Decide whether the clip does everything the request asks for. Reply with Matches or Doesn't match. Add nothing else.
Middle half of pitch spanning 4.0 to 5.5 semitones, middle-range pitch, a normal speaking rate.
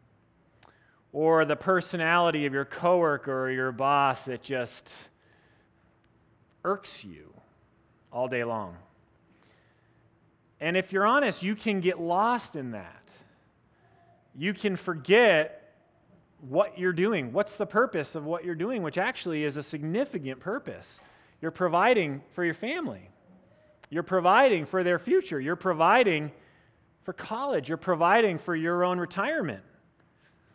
Doesn't match